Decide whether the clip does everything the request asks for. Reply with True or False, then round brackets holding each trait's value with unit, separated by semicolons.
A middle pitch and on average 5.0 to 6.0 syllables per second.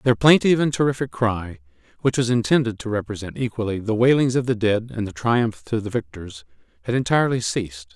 False (110 Hz; 5.9 syllables/s)